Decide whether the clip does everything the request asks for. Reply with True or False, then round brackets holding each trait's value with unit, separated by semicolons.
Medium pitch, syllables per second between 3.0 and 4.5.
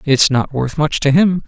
True (145 Hz; 4.4 syllables/s)